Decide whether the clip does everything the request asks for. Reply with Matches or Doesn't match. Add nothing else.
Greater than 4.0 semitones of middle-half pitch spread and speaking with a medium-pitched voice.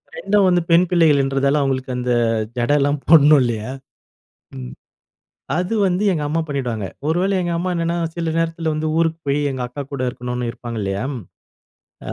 Matches